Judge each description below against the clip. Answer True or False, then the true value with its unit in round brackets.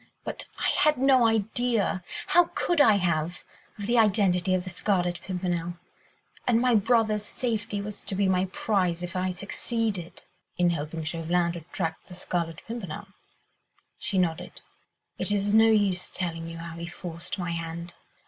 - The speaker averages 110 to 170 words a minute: True (155 wpm)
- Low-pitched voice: False (185 Hz)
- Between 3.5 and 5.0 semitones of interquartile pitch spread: True (3.9 semitones)